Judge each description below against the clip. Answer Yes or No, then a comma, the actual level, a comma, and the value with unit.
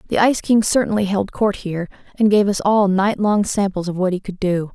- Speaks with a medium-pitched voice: No, high, 200 Hz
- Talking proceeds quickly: Yes, fast, 240 wpm